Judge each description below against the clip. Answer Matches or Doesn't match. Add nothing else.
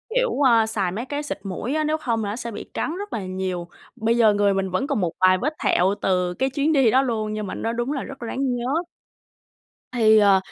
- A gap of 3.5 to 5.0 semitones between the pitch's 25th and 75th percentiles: Doesn't match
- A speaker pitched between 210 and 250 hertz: Matches